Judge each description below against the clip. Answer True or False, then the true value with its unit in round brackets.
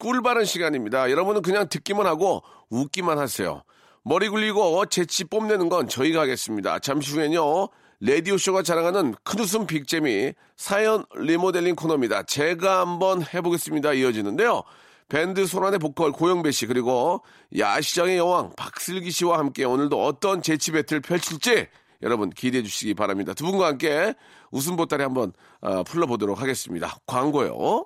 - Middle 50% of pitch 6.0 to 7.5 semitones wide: False (5.2 semitones)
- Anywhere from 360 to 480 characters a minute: True (365 characters per minute)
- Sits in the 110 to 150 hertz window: False (170 Hz)